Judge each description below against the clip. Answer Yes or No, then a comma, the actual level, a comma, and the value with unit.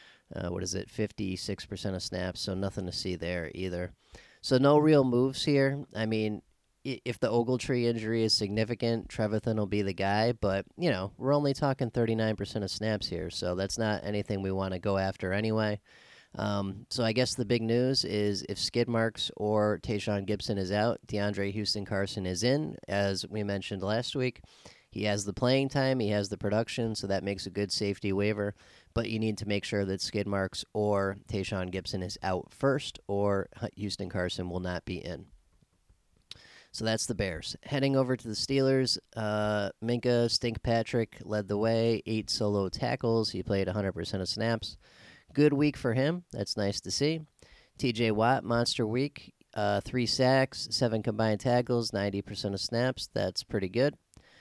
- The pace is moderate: Yes, average, 175 wpm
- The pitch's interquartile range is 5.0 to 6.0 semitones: No, average, 3.2 semitones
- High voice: No, low, 105 Hz